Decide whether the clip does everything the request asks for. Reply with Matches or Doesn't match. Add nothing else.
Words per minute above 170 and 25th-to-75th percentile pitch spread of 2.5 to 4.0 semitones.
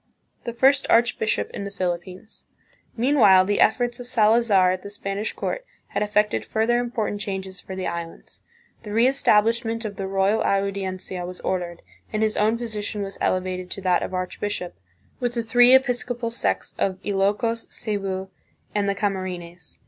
Doesn't match